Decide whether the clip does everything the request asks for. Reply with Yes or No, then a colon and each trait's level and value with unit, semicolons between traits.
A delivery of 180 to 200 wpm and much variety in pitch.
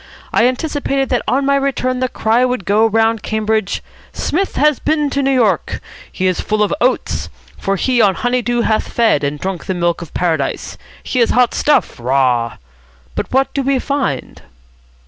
Yes: average, 185 wpm; wide, 5.8 semitones